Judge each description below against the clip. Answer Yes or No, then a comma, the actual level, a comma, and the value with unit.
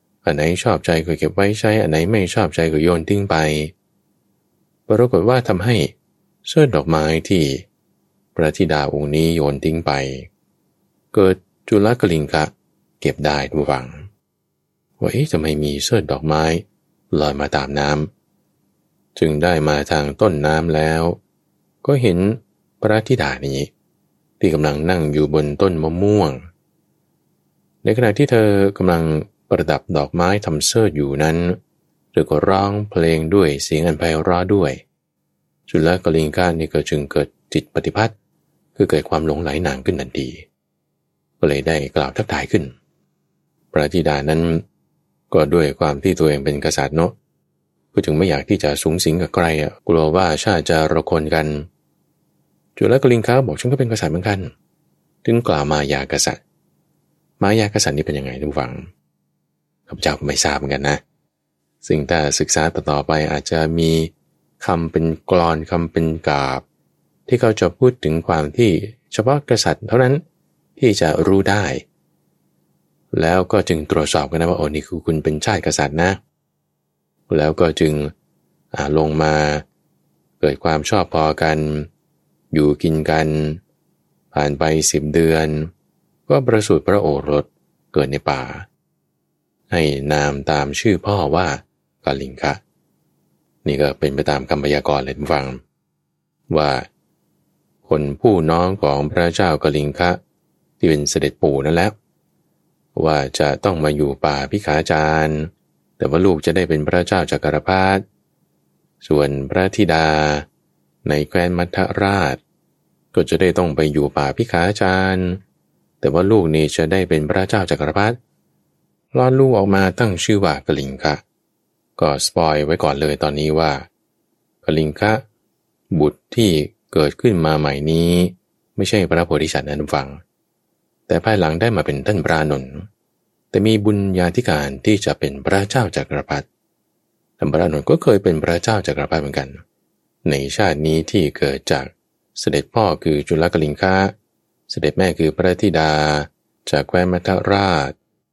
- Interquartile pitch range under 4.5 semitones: Yes, average, 4.0 semitones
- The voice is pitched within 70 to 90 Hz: Yes, very low, 80 Hz